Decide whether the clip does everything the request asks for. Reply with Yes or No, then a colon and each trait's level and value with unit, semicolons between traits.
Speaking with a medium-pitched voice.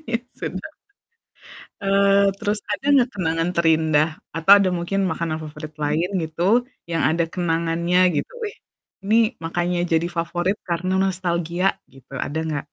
Yes: medium, 175 Hz